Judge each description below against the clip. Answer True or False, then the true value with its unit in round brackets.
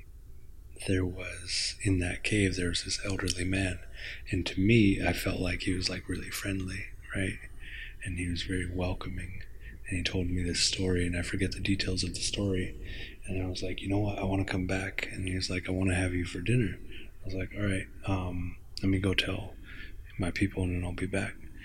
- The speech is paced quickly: True (220 wpm)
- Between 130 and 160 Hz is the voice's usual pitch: False (95 Hz)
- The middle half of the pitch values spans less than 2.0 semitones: True (1.3 semitones)